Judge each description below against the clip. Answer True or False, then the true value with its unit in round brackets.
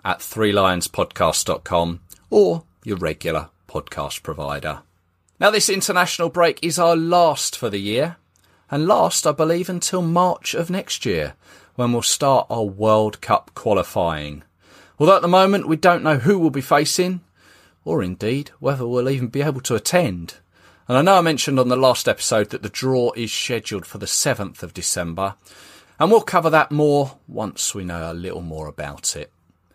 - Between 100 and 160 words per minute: False (170 wpm)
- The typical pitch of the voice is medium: False (125 Hz)